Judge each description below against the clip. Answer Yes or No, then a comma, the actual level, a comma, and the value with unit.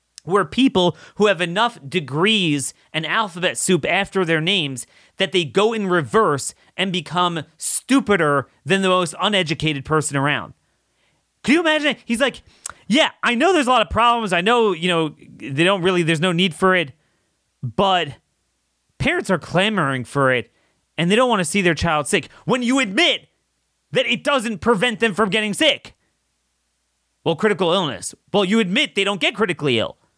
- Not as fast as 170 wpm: No, average, 175 wpm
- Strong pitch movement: Yes, wide, 6.4 semitones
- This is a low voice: No, medium, 185 Hz